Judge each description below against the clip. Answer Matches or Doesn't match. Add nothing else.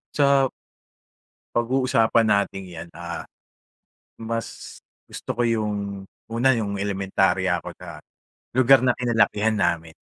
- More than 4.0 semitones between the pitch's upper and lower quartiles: Doesn't match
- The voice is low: Matches